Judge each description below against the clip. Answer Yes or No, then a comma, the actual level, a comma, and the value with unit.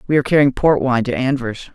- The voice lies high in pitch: No, low, 135 Hz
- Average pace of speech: No, fast, 240 wpm